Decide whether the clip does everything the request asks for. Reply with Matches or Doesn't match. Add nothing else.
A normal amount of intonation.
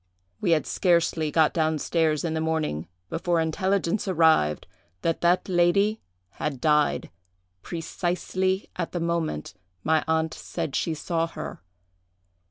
Doesn't match